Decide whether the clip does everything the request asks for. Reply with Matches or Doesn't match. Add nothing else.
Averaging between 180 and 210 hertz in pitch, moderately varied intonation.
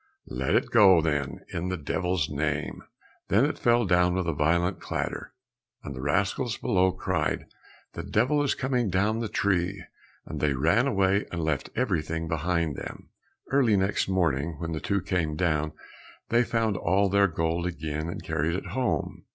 Doesn't match